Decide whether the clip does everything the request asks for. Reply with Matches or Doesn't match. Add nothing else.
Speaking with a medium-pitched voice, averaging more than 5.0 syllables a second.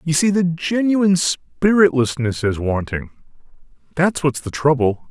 Doesn't match